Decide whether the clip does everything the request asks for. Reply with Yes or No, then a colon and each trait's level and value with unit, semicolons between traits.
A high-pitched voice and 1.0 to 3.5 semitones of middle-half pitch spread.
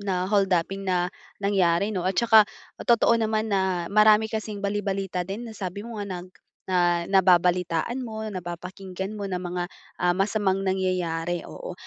Yes: high, 195 Hz; average, 2.8 semitones